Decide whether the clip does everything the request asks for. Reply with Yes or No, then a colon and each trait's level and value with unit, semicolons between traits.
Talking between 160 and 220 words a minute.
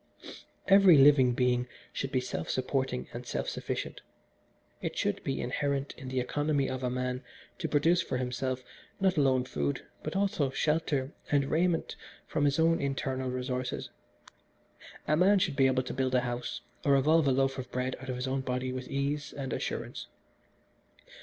Yes: average, 170 wpm